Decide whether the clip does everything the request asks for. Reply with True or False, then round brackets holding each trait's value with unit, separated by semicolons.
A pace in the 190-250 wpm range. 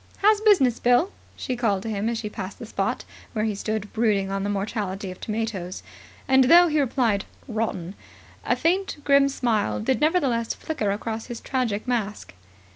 False (175 wpm)